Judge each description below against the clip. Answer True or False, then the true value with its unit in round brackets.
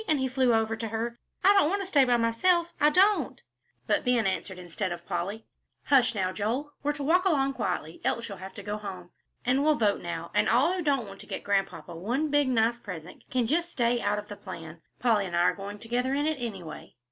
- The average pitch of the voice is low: False (235 Hz)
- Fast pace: True (235 wpm)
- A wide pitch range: True (6.4 semitones)